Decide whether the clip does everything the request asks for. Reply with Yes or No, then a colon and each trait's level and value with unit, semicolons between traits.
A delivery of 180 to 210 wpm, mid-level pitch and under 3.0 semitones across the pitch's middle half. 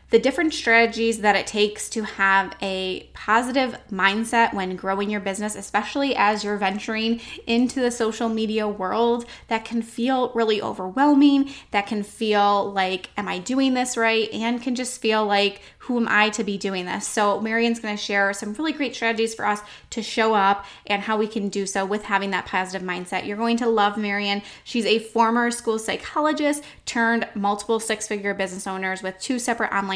No: average, 190 wpm; high, 215 Hz; narrow, 2.6 semitones